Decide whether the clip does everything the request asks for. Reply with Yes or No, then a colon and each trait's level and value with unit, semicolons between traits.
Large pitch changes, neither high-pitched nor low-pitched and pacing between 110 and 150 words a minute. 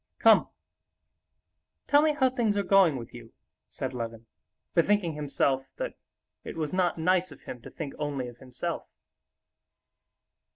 Yes: wide, 7.4 semitones; medium, 155 Hz; average, 140 wpm